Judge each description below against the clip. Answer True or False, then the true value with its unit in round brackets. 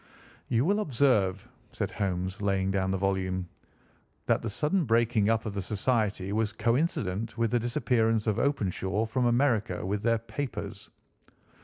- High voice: False (110 Hz)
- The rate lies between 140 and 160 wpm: True (150 wpm)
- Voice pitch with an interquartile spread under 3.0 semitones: False (3.5 semitones)